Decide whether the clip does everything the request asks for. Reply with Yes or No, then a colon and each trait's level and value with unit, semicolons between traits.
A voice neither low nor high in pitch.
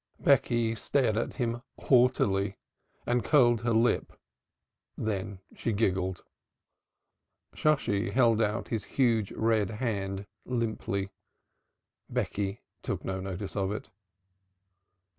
No: low, 110 Hz